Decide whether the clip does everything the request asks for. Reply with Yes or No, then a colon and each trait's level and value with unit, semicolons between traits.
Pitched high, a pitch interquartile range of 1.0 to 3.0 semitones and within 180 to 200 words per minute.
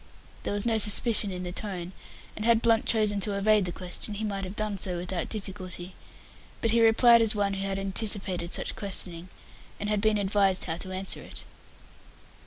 Yes: high, 200 Hz; narrow, 2.4 semitones; average, 195 wpm